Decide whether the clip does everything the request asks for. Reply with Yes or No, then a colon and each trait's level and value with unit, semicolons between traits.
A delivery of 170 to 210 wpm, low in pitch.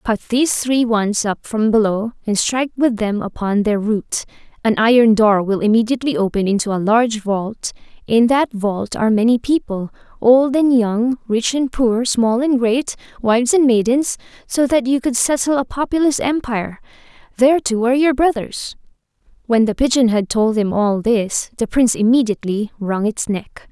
No: average, 175 wpm; high, 235 Hz